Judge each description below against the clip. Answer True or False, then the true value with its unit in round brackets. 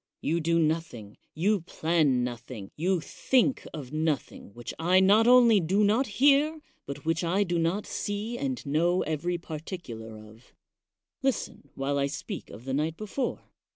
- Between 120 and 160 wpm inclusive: True (155 wpm)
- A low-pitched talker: False (165 Hz)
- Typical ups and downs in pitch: False (6.3 semitones)